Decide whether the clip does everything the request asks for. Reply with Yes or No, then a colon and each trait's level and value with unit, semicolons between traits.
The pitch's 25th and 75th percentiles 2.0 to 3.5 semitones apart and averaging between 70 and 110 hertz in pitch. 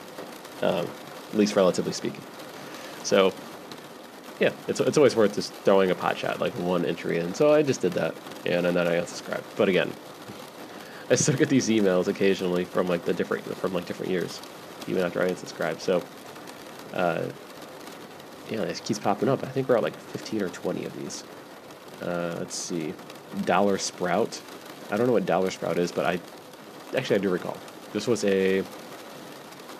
Yes: average, 3.0 semitones; very low, 95 Hz